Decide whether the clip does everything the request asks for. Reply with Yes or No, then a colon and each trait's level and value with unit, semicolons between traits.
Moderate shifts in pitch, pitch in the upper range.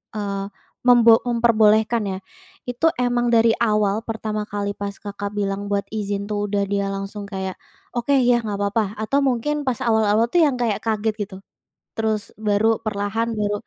No: narrow, 2.2 semitones; high, 215 Hz